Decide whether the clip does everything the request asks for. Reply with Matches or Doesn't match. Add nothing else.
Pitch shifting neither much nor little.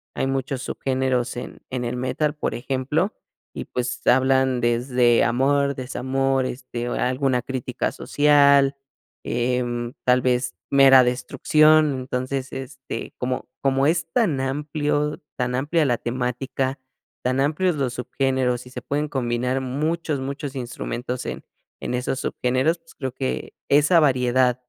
Doesn't match